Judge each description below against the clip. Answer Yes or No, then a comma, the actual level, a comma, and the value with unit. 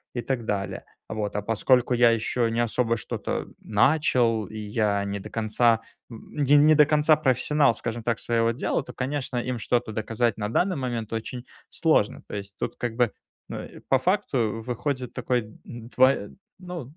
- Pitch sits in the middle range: No, low, 120 Hz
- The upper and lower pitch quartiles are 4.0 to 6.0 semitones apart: No, average, 2.9 semitones